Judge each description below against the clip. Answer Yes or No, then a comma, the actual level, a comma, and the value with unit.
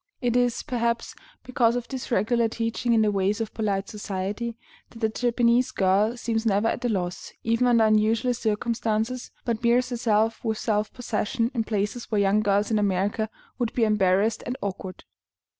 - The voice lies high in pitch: Yes, high, 225 Hz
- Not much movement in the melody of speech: Yes, narrow, 2.3 semitones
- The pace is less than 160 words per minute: No, average, 175 wpm